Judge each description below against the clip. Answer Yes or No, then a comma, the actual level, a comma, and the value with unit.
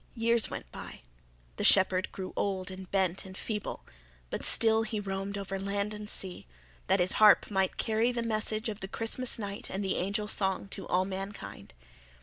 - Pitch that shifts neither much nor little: No, narrow, 2.2 semitones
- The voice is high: Yes, high, 200 Hz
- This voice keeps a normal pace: Yes, average, 180 wpm